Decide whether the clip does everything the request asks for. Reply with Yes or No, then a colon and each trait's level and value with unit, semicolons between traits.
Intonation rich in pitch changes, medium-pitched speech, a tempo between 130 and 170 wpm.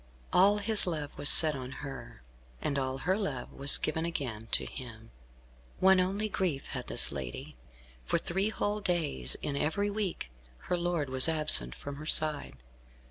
Yes: wide, 6.0 semitones; medium, 155 Hz; average, 165 wpm